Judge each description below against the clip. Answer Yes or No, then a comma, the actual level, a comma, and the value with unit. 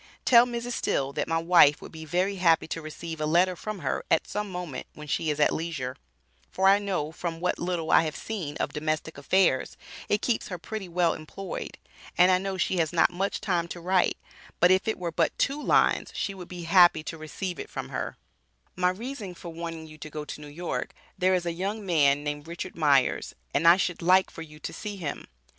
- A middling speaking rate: No, fast, 225 wpm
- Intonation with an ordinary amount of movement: Yes, average, 3.2 semitones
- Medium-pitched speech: Yes, medium, 175 Hz